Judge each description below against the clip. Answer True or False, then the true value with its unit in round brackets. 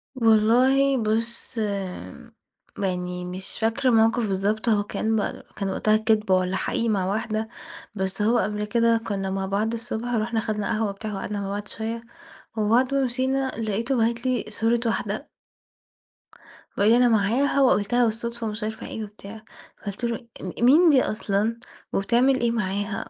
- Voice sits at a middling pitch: False (220 Hz)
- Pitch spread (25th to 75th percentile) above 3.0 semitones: False (2.6 semitones)